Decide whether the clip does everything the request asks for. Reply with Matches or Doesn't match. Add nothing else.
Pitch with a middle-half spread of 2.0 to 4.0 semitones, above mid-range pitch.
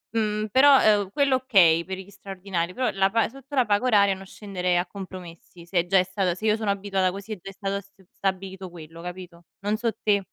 Matches